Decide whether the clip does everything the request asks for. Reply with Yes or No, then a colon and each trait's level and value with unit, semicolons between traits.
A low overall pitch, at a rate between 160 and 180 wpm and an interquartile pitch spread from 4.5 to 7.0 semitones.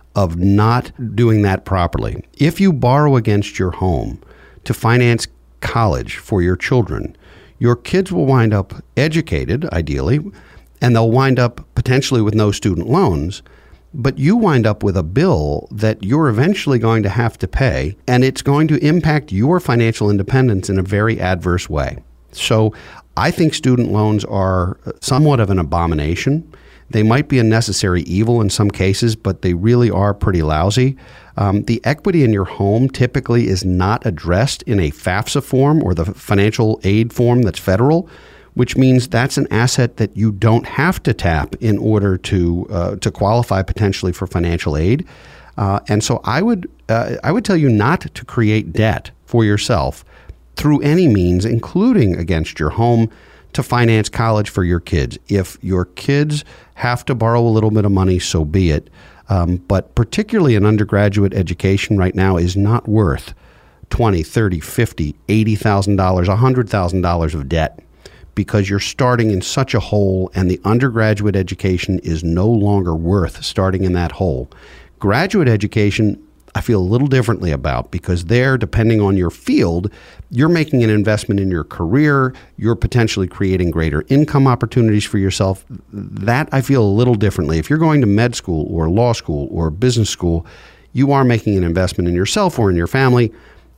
Yes: low, 105 Hz; average, 175 wpm; average, 4.9 semitones